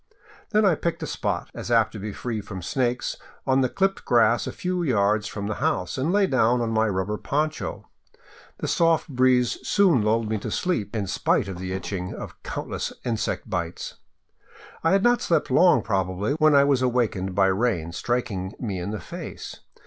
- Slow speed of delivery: No, average, 190 wpm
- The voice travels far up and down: Yes, wide, 6.0 semitones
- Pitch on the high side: No, low, 115 Hz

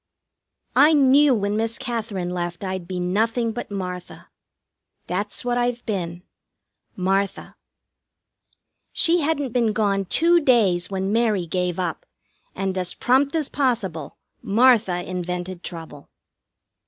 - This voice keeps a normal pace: No, slow, 120 wpm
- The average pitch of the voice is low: No, high, 200 Hz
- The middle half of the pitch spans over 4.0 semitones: Yes, average, 5.1 semitones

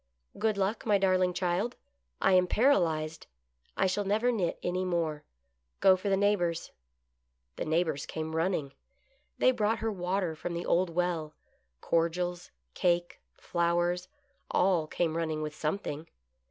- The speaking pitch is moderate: Yes, medium, 175 Hz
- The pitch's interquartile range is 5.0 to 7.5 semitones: No, average, 3.0 semitones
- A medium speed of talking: Yes, average, 150 wpm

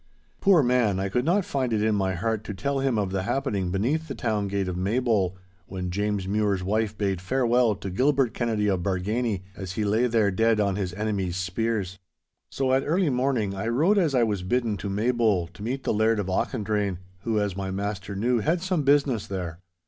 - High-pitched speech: No, low, 105 Hz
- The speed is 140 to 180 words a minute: No, fast, 205 wpm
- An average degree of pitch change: Yes, average, 4.3 semitones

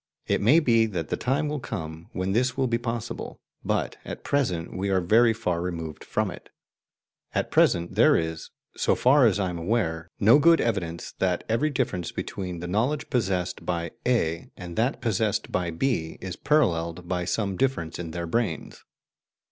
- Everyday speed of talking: Yes, average, 180 wpm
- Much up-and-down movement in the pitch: Yes, wide, 5.8 semitones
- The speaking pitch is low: Yes, very low, 95 Hz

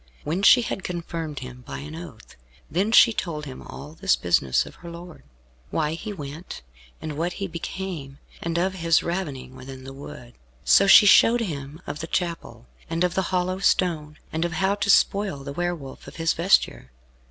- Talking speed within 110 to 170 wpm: No, average, 190 wpm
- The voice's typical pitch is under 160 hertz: No, medium, 165 Hz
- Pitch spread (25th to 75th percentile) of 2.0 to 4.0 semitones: No, average, 4.4 semitones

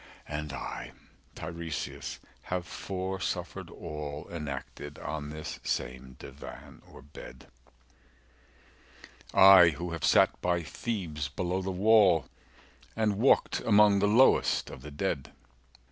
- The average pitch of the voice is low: Yes, very low, 85 Hz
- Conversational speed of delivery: No, slow, 115 wpm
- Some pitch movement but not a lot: Yes, average, 4.6 semitones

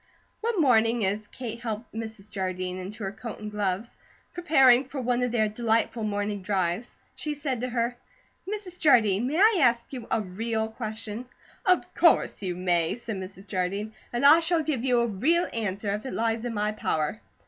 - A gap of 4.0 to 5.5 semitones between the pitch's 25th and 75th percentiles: No, average, 3.5 semitones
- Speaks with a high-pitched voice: Yes, high, 225 Hz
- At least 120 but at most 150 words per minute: No, average, 185 wpm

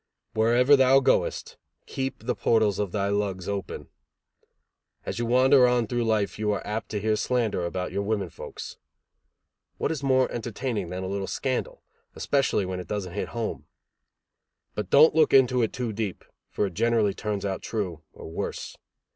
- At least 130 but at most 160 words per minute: No, average, 170 wpm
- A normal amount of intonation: Yes, average, 3.8 semitones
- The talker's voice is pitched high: No, low, 110 Hz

